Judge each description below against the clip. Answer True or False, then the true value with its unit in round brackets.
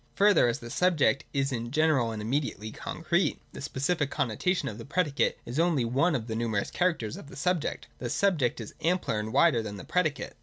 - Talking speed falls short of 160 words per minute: False (205 wpm)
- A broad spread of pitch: True (6.1 semitones)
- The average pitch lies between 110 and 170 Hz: True (135 Hz)